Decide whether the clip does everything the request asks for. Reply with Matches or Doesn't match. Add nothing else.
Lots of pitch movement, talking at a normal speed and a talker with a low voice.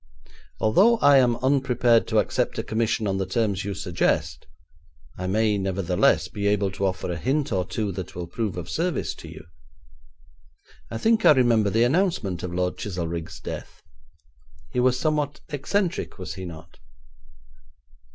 Matches